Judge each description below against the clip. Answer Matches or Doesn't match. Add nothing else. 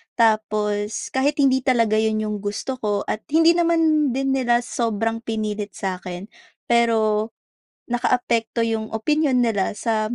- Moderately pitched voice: Doesn't match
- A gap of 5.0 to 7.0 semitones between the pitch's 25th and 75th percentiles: Doesn't match